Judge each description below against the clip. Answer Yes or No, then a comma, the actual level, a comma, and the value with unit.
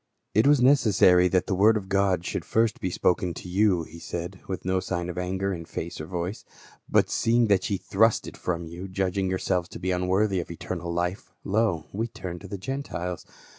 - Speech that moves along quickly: Yes, fast, 210 wpm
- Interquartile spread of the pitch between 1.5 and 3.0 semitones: Yes, narrow, 2.5 semitones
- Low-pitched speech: Yes, very low, 95 Hz